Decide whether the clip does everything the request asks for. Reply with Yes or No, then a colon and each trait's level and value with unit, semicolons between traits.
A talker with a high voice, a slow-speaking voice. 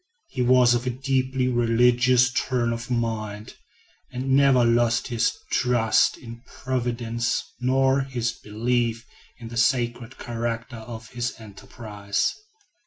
No: low, 120 Hz; slow, 120 wpm